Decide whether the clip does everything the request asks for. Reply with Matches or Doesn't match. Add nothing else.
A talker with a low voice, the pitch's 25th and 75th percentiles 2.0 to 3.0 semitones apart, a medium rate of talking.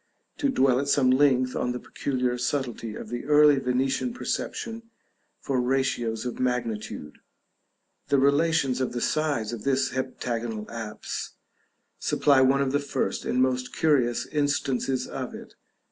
Matches